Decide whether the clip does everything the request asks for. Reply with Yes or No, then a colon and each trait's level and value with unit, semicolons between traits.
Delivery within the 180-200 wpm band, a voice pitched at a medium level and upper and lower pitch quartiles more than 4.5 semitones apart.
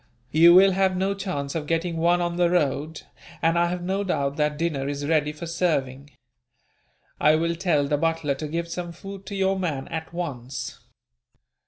No: average, 185 wpm; medium, 165 Hz; average, 3.2 semitones